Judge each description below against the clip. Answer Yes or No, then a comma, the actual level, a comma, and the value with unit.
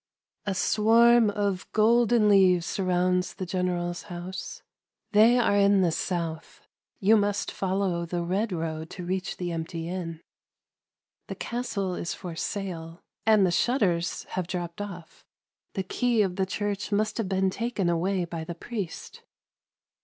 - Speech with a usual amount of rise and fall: Yes, average, 3.0 semitones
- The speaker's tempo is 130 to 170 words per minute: Yes, average, 155 wpm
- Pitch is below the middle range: No, medium, 185 Hz